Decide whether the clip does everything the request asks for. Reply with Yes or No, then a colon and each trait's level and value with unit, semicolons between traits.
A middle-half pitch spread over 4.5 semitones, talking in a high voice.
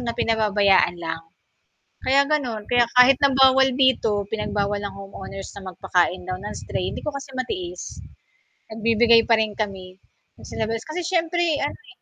Yes: average, 5.1 semitones; high, 225 Hz